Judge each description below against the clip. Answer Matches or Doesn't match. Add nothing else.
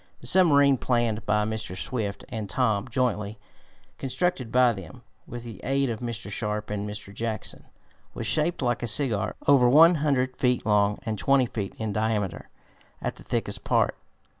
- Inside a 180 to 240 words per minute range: Doesn't match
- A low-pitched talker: Matches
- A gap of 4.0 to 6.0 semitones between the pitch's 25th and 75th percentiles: Doesn't match